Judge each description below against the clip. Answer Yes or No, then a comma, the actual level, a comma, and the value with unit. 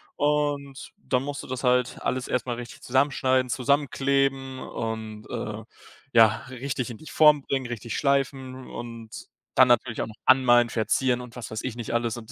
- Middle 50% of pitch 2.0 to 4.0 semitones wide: Yes, narrow, 2.5 semitones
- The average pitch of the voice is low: Yes, low, 125 Hz